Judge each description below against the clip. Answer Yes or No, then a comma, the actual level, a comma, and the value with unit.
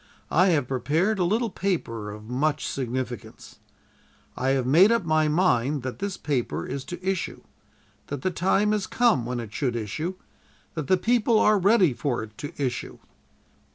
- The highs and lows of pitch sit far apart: Yes, wide, 7.0 semitones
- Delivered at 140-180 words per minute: Yes, average, 170 wpm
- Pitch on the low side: No, medium, 155 Hz